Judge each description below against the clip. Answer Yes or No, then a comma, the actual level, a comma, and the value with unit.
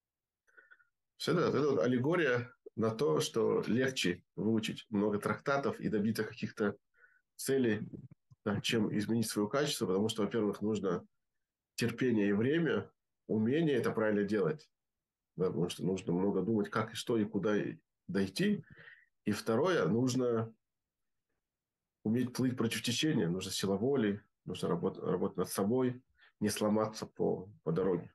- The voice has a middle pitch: No, low, 110 Hz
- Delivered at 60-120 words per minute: No, average, 130 wpm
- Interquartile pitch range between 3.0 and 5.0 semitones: Yes, average, 3.4 semitones